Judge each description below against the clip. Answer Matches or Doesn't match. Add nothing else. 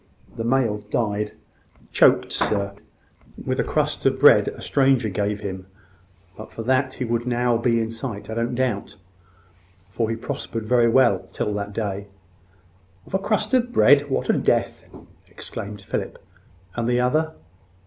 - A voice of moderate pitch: Doesn't match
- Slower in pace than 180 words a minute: Matches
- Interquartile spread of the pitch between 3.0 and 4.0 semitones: Matches